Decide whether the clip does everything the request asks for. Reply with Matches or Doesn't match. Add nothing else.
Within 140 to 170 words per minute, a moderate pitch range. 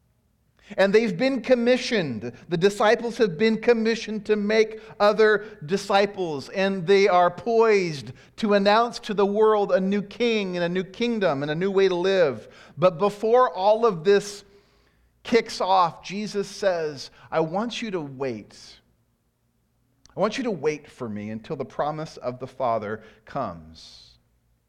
Doesn't match